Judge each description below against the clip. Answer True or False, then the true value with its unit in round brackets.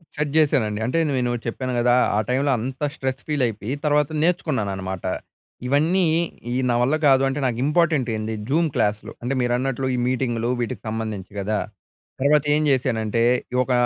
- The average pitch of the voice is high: False (125 Hz)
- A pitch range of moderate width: True (4.1 semitones)